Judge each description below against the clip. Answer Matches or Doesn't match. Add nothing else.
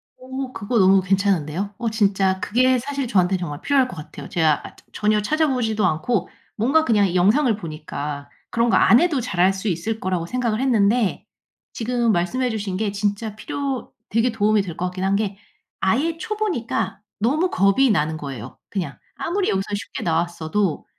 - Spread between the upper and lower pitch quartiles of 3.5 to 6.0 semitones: Matches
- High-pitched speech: Matches